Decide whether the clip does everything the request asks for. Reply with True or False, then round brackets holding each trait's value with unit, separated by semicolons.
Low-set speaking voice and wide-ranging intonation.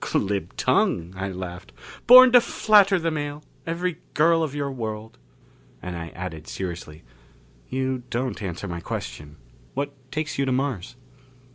True (130 Hz; 9.0 semitones)